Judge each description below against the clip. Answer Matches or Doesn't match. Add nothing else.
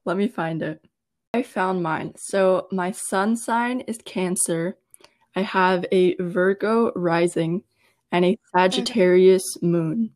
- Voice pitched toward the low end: Doesn't match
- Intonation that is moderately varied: Doesn't match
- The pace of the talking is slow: Matches